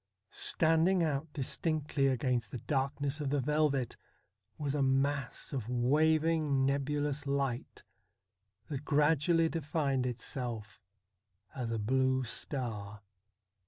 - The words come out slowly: Yes, slow, 110 wpm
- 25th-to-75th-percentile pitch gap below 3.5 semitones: Yes, average, 2.8 semitones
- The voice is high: No, medium, 140 Hz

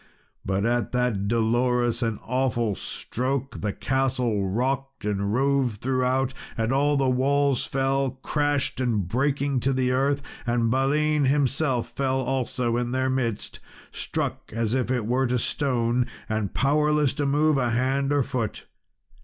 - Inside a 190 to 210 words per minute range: No, average, 145 wpm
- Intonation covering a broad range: No, narrow, 2.5 semitones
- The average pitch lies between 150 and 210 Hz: No, low, 130 Hz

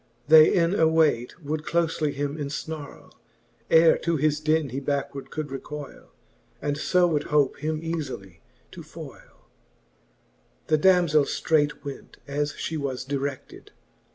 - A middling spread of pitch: No, narrow, 2.1 semitones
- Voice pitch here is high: No, medium, 150 Hz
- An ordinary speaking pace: No, slow, 130 wpm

